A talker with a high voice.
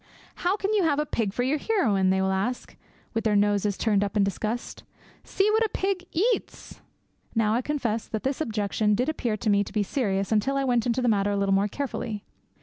Yes: high, 225 Hz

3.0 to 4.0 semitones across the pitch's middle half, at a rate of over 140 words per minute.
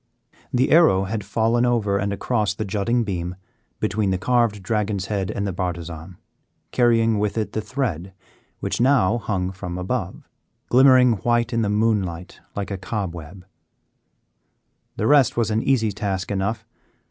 Yes: average, 3.7 semitones; average, 150 wpm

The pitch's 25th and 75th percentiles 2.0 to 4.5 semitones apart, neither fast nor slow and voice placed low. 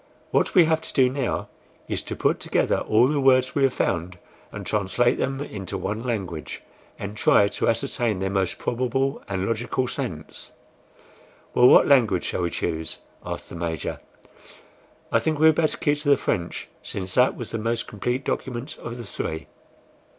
No: wide, 5.6 semitones; average, 180 wpm; low, 115 Hz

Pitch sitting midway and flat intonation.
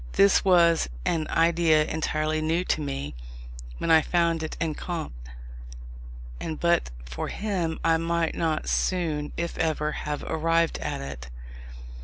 Yes: medium, 160 Hz; narrow, 1.6 semitones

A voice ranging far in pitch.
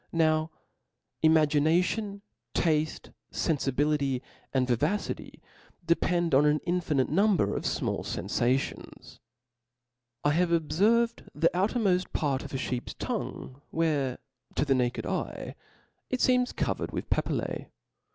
No: average, 4.7 semitones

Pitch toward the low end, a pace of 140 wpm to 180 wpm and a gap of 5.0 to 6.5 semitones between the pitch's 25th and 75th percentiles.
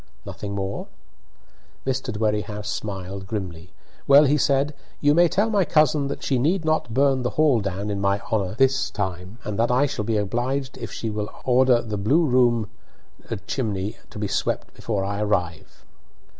Yes: low, 115 Hz; average, 170 wpm; average, 5.3 semitones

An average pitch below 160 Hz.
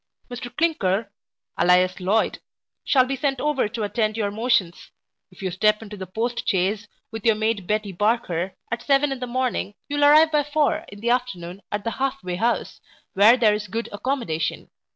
No: high, 225 Hz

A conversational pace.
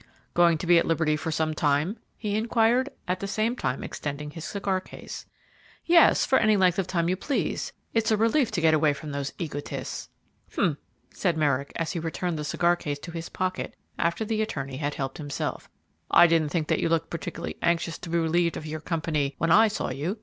No: fast, 210 wpm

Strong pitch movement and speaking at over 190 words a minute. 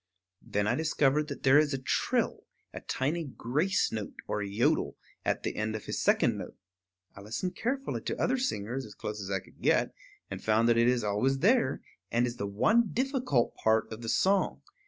Yes: wide, 7.6 semitones; average, 200 wpm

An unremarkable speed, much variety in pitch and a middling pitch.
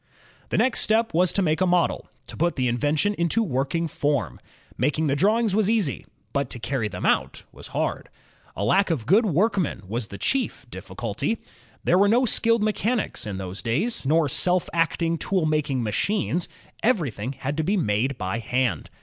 Yes: average, 180 wpm; wide, 7.9 semitones; medium, 160 Hz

